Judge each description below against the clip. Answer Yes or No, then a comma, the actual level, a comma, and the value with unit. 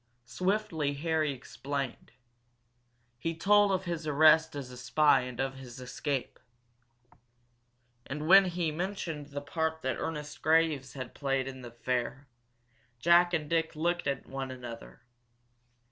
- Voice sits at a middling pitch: Yes, medium, 150 Hz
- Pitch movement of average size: Yes, average, 3.7 semitones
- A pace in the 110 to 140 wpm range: Yes, slow, 135 wpm